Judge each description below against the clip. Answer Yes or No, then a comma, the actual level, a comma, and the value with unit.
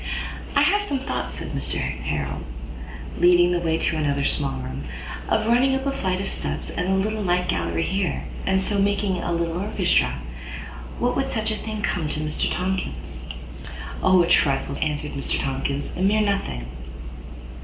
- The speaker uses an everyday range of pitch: No, wide, 6.1 semitones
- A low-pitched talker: No, medium, 175 Hz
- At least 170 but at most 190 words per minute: Yes, average, 175 wpm